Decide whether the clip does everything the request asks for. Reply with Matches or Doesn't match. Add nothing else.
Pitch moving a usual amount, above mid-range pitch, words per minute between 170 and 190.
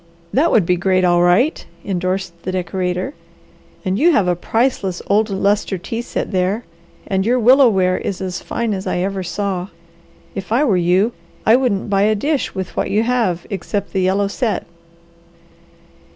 Matches